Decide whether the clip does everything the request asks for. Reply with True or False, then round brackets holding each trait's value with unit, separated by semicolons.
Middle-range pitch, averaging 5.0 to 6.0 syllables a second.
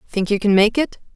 False (210 Hz; 5.8 syllables/s)